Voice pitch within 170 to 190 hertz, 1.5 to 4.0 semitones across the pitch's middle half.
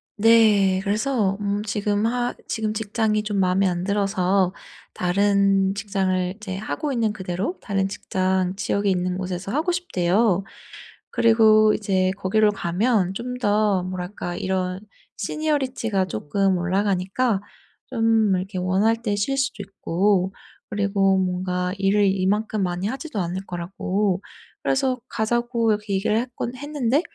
No: high, 200 Hz; average, 2.9 semitones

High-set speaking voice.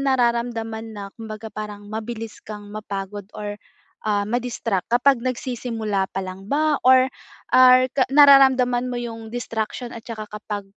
Yes: high, 225 Hz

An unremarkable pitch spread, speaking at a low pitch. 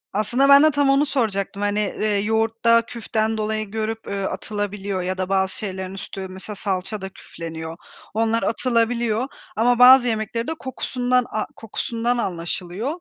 No: average, 3.5 semitones; high, 220 Hz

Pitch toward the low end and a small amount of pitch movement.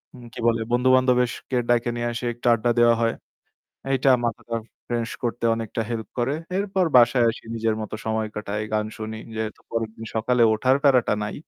Yes: low, 120 Hz; narrow, 1.9 semitones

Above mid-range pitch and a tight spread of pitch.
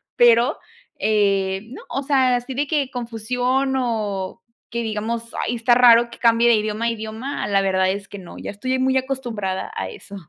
No: high, 235 Hz; average, 3.3 semitones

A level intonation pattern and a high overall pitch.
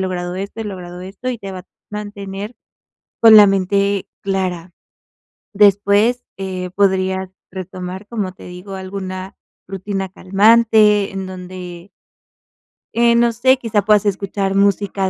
Yes: narrow, 1.9 semitones; high, 195 Hz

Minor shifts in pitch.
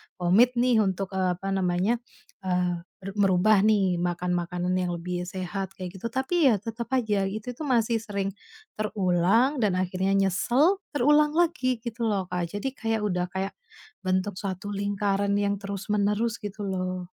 No: average, 3.4 semitones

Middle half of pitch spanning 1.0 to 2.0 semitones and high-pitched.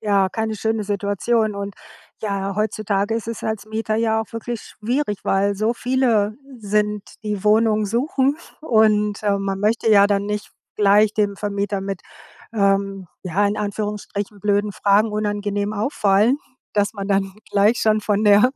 Yes: narrow, 1.5 semitones; high, 210 Hz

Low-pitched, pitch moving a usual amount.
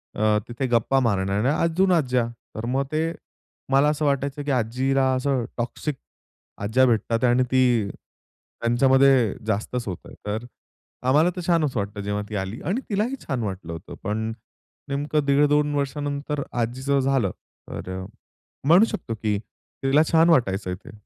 Yes: low, 130 Hz; average, 4.6 semitones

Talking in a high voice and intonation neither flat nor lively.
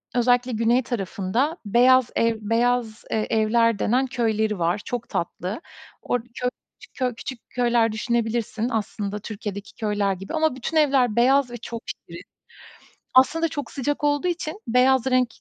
Yes: high, 235 Hz; average, 3.0 semitones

